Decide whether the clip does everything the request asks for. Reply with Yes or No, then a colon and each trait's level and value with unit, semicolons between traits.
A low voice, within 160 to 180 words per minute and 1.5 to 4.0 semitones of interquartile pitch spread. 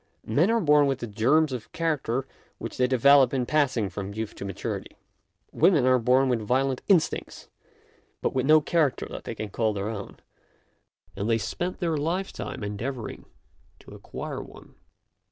No: low, 130 Hz; average, 170 wpm; average, 5.2 semitones